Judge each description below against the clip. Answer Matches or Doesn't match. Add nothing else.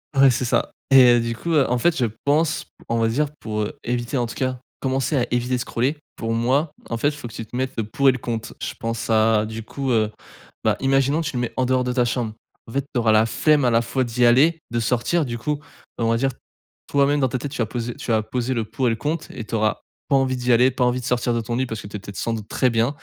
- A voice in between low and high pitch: Doesn't match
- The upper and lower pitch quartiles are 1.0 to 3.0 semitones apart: Matches